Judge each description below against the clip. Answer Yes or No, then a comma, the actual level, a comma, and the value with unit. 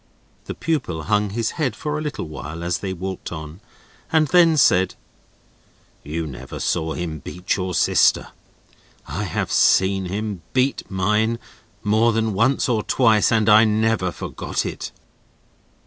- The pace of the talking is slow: No, average, 150 wpm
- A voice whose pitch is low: Yes, low, 105 Hz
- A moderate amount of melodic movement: Yes, average, 4.4 semitones